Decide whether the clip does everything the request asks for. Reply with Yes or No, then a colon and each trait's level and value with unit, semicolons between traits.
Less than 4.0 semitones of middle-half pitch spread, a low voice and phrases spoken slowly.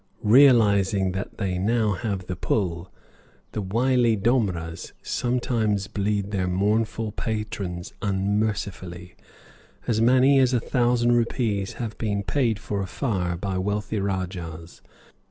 Yes: average, 3.4 semitones; low, 105 Hz; slow, 120 wpm